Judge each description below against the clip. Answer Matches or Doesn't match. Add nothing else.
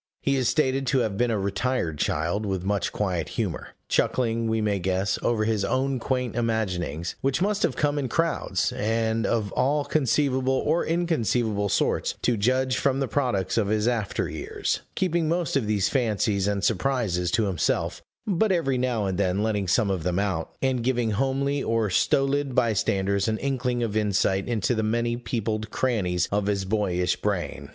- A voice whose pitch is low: Matches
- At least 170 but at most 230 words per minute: Matches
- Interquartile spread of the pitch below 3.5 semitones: Doesn't match